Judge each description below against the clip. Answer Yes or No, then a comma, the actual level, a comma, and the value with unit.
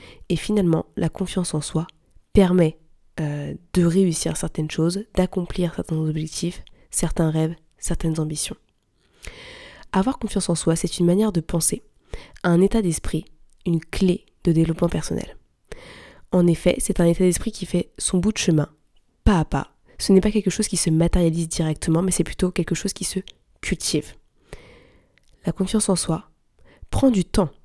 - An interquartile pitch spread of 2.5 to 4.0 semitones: Yes, average, 2.8 semitones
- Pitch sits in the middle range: Yes, medium, 175 Hz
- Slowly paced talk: No, average, 165 wpm